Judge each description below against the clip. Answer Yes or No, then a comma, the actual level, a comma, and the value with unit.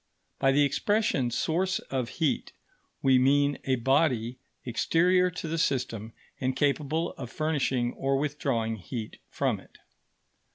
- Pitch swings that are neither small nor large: Yes, average, 4.1 semitones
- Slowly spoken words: Yes, slow, 130 wpm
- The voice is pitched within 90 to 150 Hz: Yes, low, 135 Hz